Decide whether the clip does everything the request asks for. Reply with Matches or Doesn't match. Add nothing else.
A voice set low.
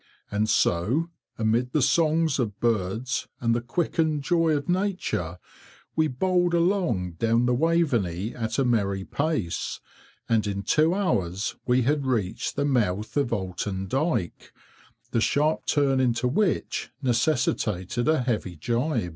Matches